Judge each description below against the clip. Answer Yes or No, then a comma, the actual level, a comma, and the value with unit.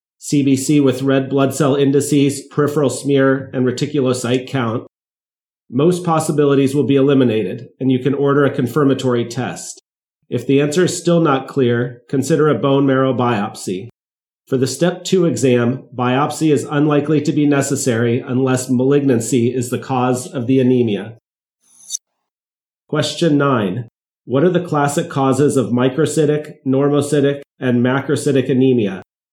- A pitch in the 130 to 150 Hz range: Yes, low, 135 Hz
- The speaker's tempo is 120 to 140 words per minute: Yes, slow, 135 wpm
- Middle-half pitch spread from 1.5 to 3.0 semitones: Yes, narrow, 2.4 semitones